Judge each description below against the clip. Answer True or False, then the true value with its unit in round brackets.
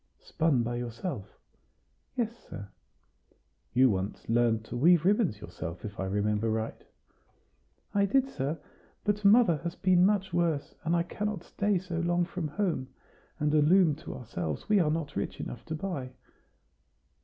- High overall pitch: False (160 Hz)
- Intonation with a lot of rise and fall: True (7.9 semitones)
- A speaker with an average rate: True (155 wpm)